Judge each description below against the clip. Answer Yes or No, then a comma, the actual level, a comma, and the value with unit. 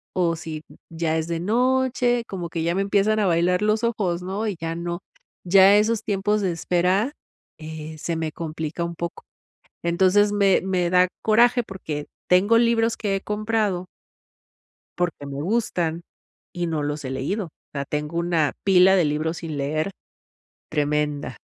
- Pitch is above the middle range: No, medium, 175 Hz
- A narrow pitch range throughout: No, average, 4.3 semitones